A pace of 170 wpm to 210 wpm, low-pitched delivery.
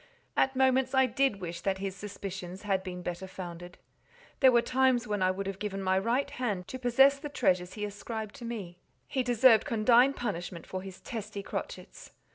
No: average, 190 wpm; high, 210 Hz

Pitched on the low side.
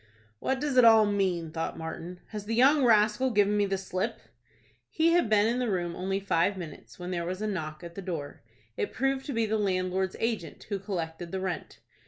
No: high, 195 Hz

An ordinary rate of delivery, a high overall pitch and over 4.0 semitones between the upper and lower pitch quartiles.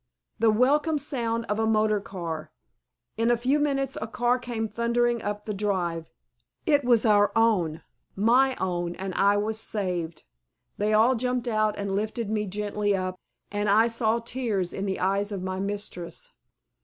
No: average, 165 wpm; high, 215 Hz; average, 3.1 semitones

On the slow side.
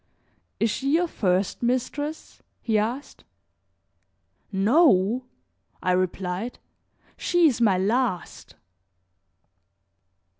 Yes: slow, 80 wpm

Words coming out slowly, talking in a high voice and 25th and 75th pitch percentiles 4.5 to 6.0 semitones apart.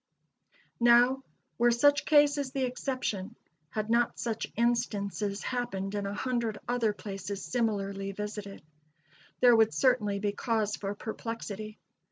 No: slow, 125 wpm; high, 220 Hz; average, 3.3 semitones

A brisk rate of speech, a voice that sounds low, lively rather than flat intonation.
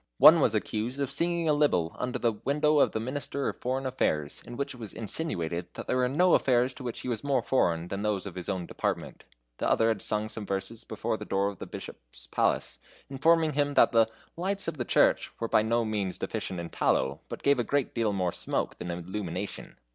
Yes: fast, 225 wpm; low, 115 Hz; wide, 6.2 semitones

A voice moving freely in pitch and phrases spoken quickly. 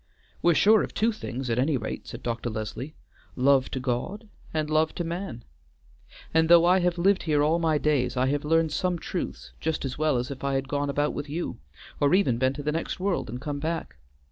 No: average, 4.3 semitones; fast, 220 wpm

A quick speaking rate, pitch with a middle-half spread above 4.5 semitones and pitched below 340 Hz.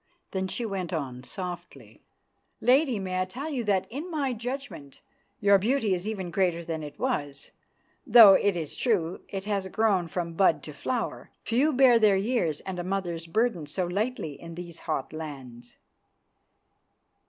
No: average, 165 wpm; wide, 5.5 semitones; high, 190 Hz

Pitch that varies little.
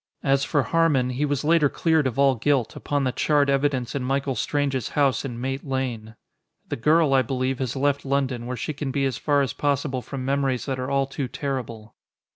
Yes: narrow, 1.9 semitones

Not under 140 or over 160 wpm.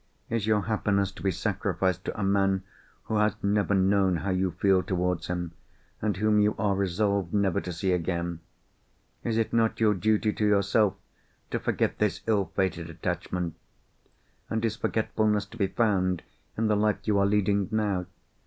No: average, 170 wpm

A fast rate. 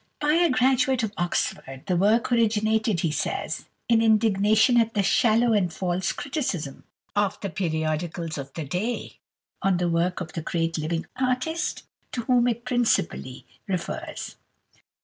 No: average, 150 wpm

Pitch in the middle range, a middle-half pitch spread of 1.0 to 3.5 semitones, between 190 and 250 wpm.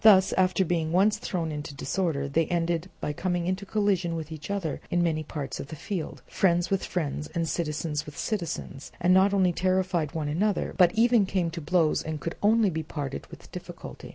Yes: medium, 170 Hz; average, 3.2 semitones; average, 200 wpm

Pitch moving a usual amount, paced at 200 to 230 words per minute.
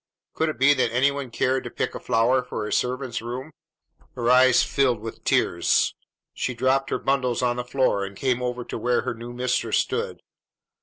No: narrow, 1.6 semitones; fast, 205 wpm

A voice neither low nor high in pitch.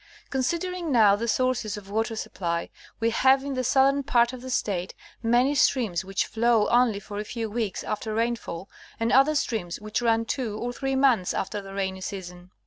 No: high, 230 Hz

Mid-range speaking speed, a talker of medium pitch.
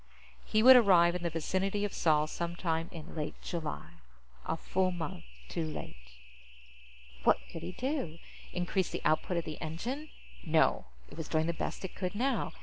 Yes: average, 175 wpm; medium, 170 Hz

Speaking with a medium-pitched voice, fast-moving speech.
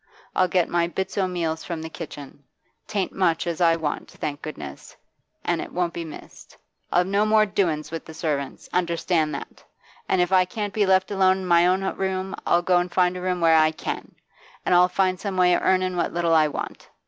Yes: medium, 180 Hz; fast, 215 wpm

